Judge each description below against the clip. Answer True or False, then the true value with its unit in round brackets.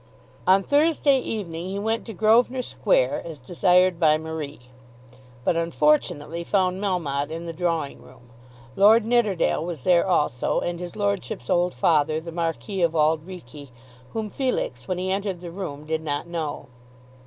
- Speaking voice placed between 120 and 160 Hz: False (170 Hz)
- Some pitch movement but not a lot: True (4.1 semitones)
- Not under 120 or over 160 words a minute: True (155 wpm)